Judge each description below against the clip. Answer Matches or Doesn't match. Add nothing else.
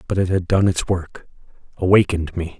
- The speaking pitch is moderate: Doesn't match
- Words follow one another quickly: Doesn't match